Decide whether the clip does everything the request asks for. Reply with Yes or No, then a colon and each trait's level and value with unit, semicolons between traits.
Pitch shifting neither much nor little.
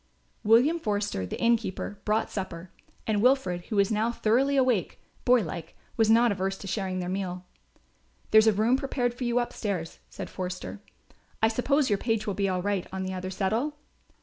Yes: average, 4.1 semitones